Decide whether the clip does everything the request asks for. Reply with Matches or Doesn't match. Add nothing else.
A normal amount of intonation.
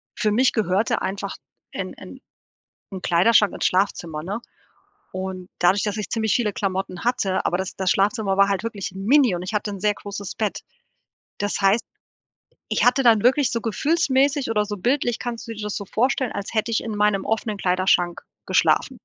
Matches